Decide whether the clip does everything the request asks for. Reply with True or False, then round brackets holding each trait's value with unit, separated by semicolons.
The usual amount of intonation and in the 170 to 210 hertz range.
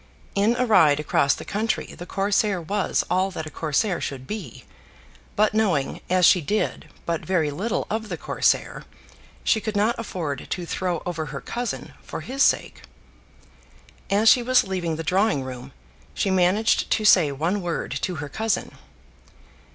True (4.9 semitones; 185 Hz)